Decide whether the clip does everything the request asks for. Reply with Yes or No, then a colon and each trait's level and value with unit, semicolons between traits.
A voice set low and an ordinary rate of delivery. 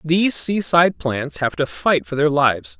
No: medium, 145 Hz; average, 195 wpm